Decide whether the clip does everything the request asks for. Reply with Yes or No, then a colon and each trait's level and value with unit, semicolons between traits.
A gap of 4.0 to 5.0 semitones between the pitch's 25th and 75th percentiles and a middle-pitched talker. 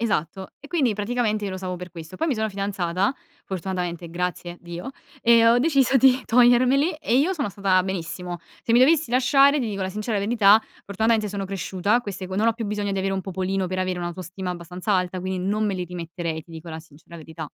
No: average, 4.3 semitones; high, 195 Hz